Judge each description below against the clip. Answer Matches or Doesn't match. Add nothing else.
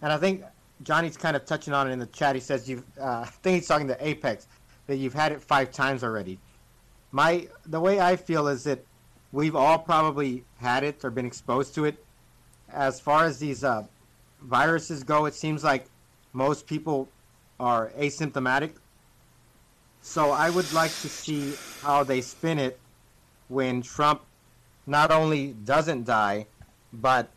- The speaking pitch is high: Doesn't match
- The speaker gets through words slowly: Doesn't match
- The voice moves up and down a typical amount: Matches